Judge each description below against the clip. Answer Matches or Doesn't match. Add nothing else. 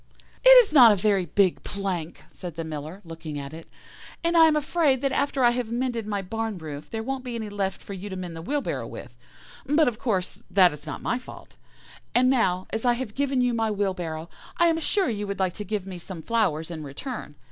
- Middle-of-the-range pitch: Doesn't match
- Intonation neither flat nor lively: Doesn't match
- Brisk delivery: Matches